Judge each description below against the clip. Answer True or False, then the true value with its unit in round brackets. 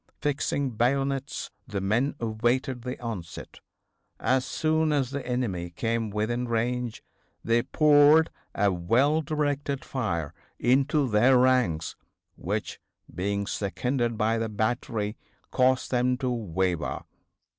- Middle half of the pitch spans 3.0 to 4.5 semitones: True (4.0 semitones)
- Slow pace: True (115 wpm)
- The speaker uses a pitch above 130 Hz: False (120 Hz)